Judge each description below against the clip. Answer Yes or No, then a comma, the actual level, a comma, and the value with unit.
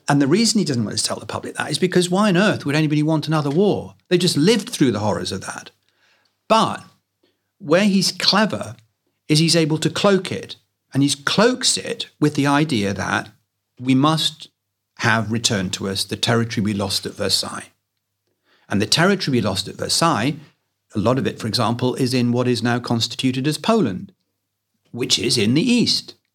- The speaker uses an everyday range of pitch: No, wide, 7.0 semitones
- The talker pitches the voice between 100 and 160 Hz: Yes, low, 135 Hz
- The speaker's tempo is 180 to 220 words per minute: Yes, average, 195 wpm